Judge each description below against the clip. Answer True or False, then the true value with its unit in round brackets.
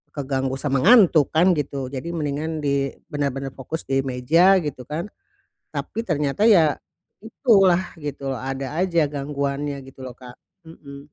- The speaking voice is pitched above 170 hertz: False (145 Hz)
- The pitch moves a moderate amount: True (3.3 semitones)